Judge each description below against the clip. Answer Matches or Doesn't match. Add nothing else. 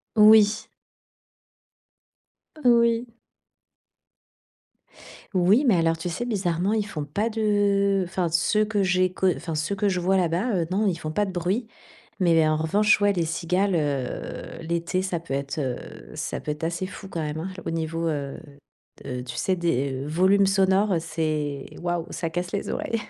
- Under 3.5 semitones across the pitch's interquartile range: Doesn't match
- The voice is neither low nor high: Matches